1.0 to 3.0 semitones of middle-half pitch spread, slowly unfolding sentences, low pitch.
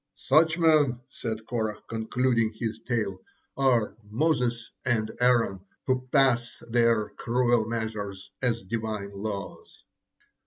Yes: narrow, 2.5 semitones; slow, 110 wpm; low, 115 Hz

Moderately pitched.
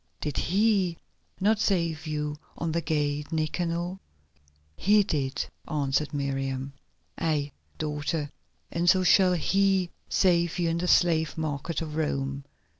Yes: medium, 160 Hz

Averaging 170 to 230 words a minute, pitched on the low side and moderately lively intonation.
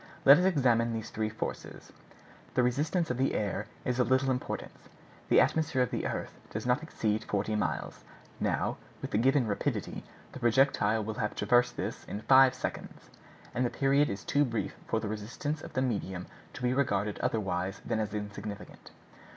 Yes: average, 180 wpm; low, 120 Hz; average, 3.8 semitones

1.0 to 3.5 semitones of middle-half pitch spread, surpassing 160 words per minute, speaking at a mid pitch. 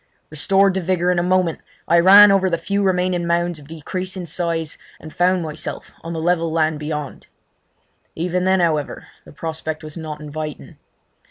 Yes: narrow, 2.6 semitones; average, 170 wpm; medium, 170 Hz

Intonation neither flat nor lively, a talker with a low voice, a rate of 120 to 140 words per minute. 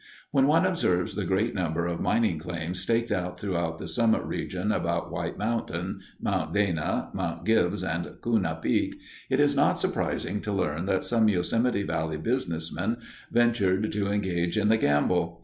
No: average, 4.7 semitones; very low, 95 Hz; average, 165 wpm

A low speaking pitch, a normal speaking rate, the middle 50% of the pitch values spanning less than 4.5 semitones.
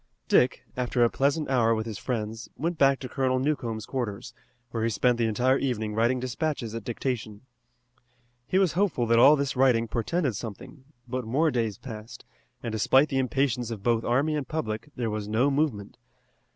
Yes: low, 125 Hz; average, 180 wpm; average, 3.4 semitones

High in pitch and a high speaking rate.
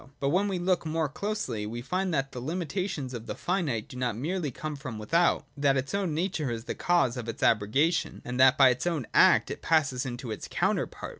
No: medium, 140 Hz; fast, 220 wpm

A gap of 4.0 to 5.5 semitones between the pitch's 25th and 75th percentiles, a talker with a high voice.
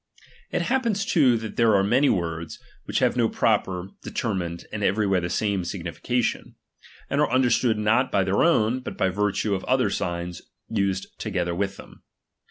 No: average, 4.7 semitones; low, 100 Hz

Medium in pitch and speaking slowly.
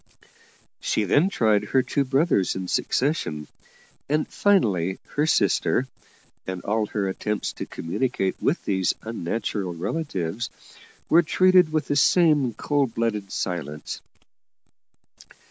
No: low, 115 Hz; slow, 115 wpm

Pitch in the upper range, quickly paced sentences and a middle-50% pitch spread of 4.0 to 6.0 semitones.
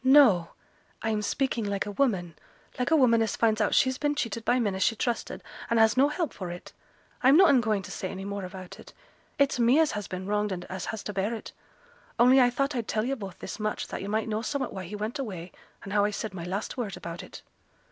Yes: high, 215 Hz; fast, 250 wpm; average, 4.3 semitones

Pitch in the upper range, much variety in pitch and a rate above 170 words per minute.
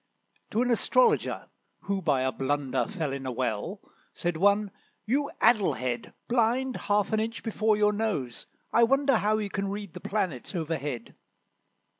No: high, 205 Hz; wide, 7.4 semitones; average, 160 wpm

